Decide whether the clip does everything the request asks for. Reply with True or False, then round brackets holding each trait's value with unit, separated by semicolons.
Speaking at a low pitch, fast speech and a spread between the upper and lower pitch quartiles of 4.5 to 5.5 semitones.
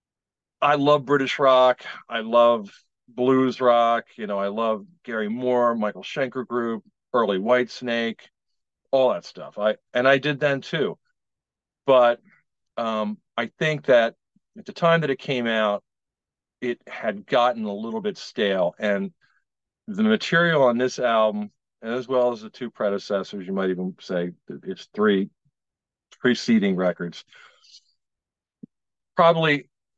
False (125 Hz; 135 wpm; 5.0 semitones)